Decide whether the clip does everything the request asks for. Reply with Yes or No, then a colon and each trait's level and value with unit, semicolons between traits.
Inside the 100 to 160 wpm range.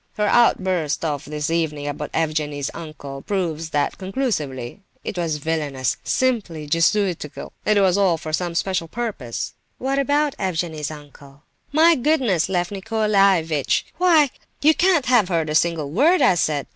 Yes: average, 150 wpm